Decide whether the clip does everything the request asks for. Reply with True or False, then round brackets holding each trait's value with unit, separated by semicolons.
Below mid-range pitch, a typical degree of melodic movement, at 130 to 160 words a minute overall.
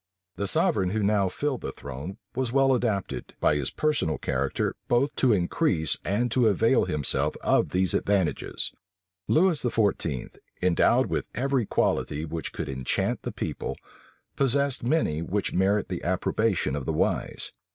False (100 Hz; 7.1 semitones; 150 wpm)